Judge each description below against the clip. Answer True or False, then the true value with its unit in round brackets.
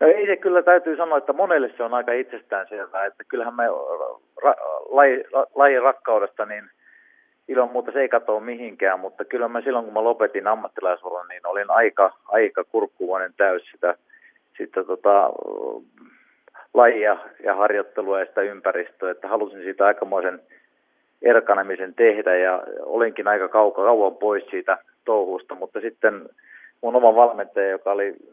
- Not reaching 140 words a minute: False (150 wpm)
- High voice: True (195 Hz)